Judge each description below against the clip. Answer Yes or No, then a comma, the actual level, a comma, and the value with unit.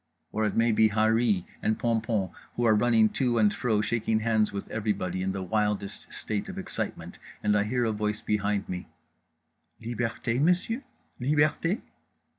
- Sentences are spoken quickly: No, average, 160 wpm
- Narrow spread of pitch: Yes, narrow, 2.2 semitones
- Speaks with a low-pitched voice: Yes, low, 110 Hz